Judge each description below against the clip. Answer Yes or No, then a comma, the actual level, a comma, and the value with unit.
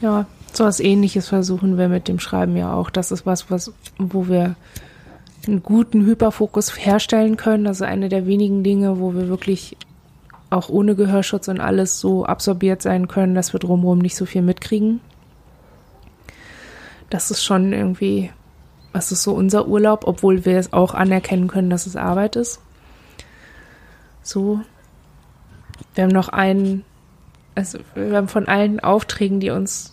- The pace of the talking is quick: No, average, 155 wpm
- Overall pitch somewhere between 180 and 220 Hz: Yes, high, 190 Hz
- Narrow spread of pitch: Yes, narrow, 2.0 semitones